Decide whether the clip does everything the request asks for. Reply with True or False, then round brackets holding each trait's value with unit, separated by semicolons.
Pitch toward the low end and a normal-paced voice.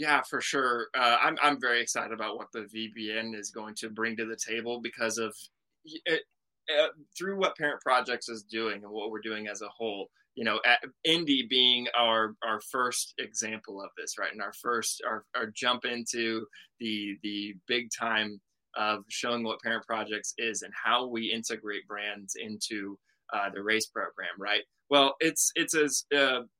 True (115 Hz; 180 wpm)